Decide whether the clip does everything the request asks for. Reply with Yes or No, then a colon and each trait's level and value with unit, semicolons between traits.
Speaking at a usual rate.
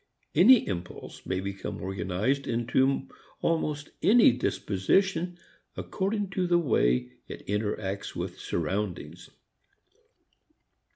No: slow, 95 wpm